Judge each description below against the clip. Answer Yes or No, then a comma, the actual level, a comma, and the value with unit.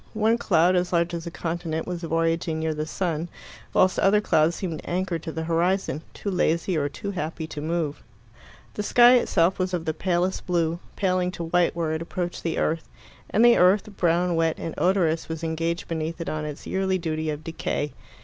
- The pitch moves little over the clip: Yes, narrow, 2.2 semitones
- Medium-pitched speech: Yes, medium, 170 Hz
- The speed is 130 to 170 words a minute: No, average, 195 wpm